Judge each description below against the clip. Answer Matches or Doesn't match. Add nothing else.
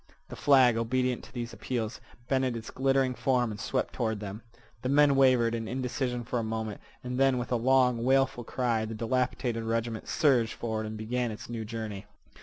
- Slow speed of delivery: Doesn't match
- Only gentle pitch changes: Matches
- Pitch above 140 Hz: Doesn't match